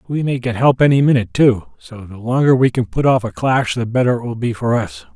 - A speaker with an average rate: No, fast, 270 wpm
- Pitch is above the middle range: No, low, 120 Hz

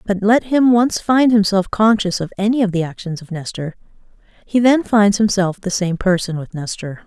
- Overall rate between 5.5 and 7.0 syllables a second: No, 5.0 syllables/s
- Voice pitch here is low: No, high, 200 Hz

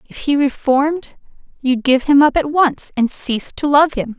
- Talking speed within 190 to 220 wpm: Yes, average, 200 wpm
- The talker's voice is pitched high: Yes, very high, 275 Hz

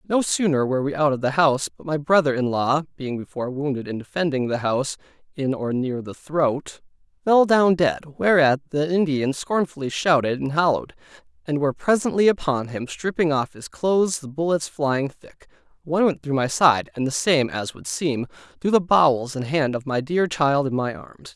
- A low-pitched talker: No, medium, 145 Hz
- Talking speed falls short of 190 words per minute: No, average, 200 wpm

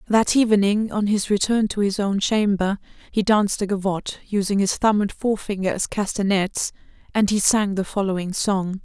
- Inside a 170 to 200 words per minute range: Yes, average, 175 wpm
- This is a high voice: Yes, high, 200 Hz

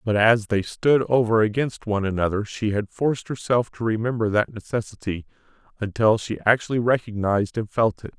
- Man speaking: Yes, male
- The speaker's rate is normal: Yes, average, 170 wpm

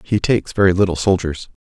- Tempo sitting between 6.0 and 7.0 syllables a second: Yes, 6.3 syllables/s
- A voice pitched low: Yes, very low, 95 Hz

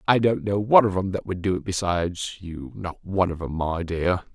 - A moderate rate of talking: No, fast, 250 wpm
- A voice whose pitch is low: Yes, very low, 95 Hz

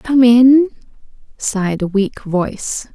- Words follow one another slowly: Yes, slow, 120 wpm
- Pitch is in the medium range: No, high, 230 Hz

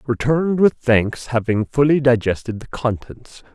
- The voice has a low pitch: Yes, low, 125 Hz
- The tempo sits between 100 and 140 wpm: Yes, slow, 135 wpm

